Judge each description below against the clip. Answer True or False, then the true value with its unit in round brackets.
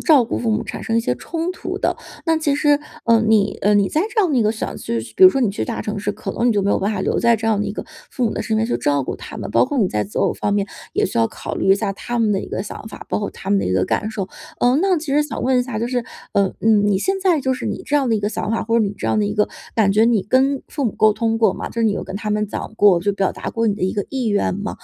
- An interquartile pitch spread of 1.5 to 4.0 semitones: True (3.4 semitones)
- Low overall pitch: False (220 Hz)